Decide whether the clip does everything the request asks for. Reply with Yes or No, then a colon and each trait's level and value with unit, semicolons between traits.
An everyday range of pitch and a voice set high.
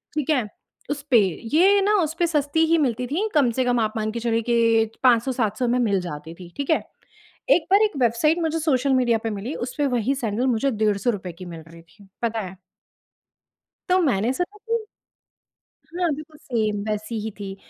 No: wide, 6.0 semitones; high, 240 Hz